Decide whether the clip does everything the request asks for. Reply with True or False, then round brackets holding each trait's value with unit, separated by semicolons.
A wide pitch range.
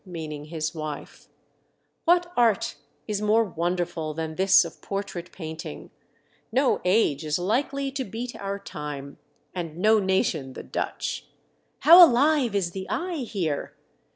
True (6.3 semitones)